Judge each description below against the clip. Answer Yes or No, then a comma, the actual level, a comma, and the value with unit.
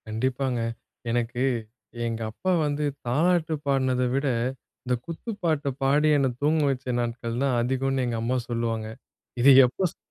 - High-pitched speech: No, low, 130 Hz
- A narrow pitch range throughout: No, average, 3.2 semitones